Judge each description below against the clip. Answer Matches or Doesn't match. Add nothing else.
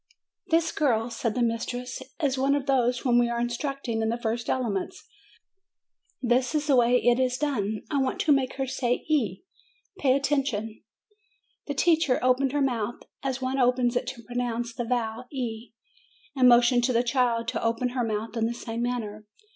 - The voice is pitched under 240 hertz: Doesn't match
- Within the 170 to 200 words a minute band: Matches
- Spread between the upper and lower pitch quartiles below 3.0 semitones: Matches